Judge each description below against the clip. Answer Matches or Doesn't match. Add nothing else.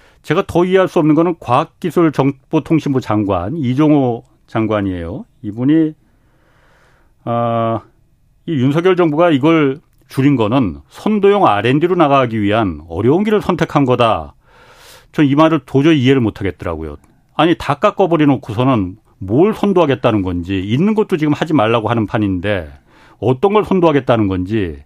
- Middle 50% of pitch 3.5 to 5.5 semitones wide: Doesn't match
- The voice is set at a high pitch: Doesn't match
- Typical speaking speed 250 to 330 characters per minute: Matches